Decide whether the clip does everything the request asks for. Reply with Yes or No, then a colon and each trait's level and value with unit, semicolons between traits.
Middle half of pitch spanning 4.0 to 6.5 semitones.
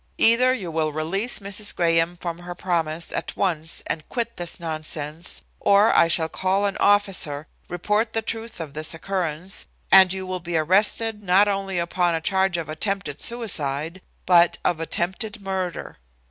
No: average, 3.4 semitones